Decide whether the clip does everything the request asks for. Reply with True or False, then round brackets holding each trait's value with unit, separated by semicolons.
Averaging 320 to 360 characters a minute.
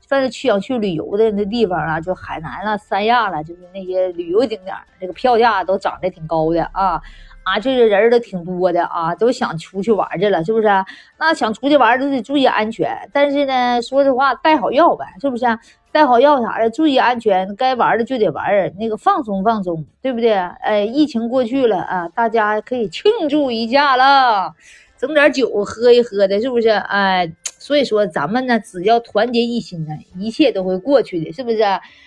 False (300 characters per minute)